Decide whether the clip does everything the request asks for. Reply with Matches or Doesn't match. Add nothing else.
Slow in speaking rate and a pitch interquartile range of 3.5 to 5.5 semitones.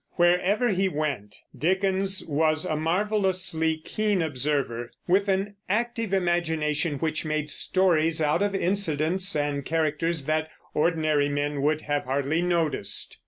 Matches